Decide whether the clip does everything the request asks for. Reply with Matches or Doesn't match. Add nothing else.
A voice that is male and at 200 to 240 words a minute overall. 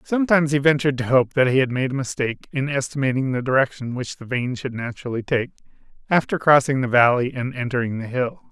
Matches